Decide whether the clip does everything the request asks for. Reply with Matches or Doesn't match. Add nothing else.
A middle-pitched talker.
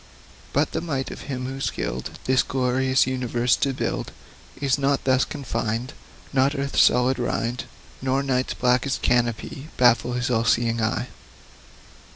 Doesn't match